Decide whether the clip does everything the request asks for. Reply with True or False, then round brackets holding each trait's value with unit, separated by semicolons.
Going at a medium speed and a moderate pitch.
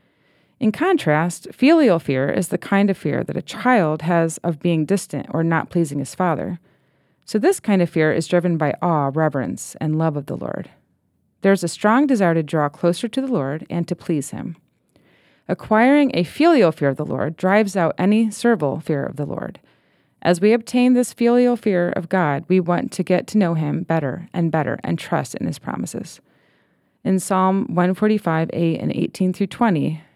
True (195 wpm; 175 Hz)